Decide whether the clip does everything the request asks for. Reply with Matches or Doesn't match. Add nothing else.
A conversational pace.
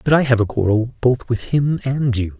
Doesn't match